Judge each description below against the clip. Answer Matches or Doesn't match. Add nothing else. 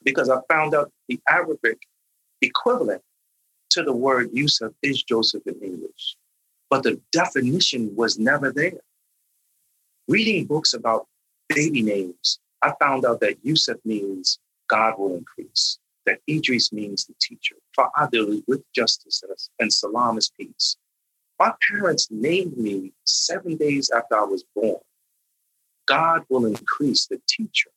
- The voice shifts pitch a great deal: Matches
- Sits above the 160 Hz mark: Doesn't match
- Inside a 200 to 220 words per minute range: Doesn't match